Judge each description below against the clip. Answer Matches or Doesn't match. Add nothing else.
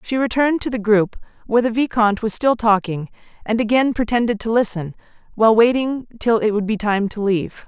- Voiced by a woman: Matches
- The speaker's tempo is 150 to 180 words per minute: Doesn't match